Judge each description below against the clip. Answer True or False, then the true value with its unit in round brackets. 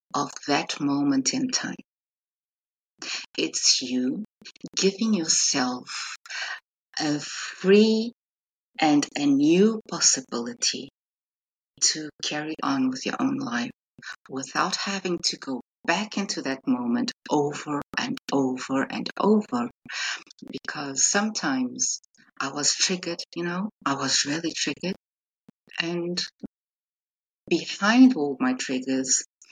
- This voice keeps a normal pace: False (105 wpm)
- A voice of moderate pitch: True (175 Hz)